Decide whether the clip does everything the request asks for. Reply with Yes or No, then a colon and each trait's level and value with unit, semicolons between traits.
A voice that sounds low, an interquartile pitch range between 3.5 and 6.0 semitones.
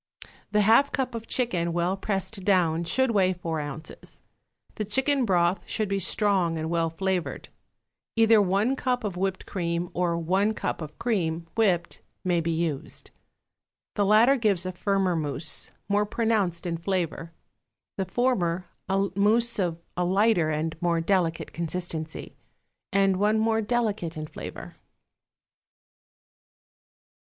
No: high, 190 Hz; average, 4.0 semitones